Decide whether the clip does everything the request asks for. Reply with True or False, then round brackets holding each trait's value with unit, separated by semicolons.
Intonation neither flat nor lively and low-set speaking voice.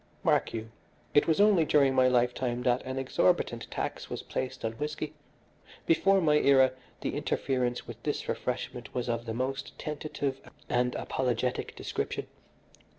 True (3.1 semitones; 130 Hz)